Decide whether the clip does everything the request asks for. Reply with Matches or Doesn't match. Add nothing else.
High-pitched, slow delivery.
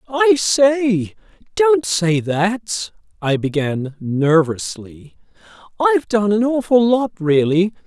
Matches